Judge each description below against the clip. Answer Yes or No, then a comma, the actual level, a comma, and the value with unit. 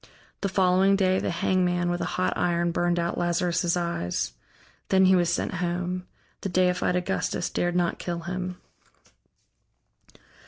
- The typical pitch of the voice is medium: Yes, medium, 180 Hz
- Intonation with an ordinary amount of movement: No, narrow, 1.0 semitones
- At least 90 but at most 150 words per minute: Yes, average, 145 wpm